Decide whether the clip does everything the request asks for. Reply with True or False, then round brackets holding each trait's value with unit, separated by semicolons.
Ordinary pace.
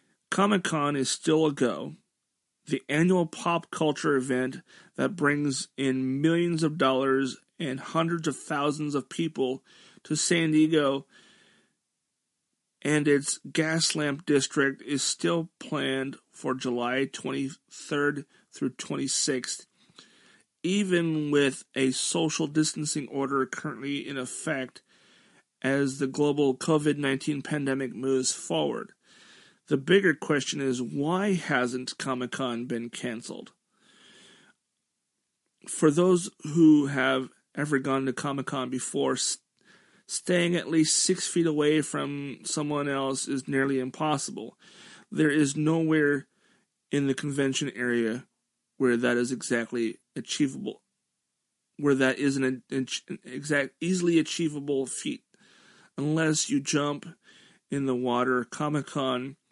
False (115 wpm)